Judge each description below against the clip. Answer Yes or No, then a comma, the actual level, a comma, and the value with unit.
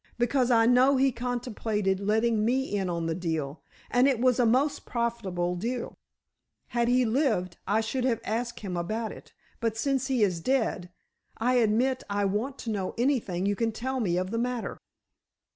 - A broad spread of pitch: No, average, 3.8 semitones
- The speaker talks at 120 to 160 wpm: No, average, 180 wpm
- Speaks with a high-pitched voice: Yes, high, 230 Hz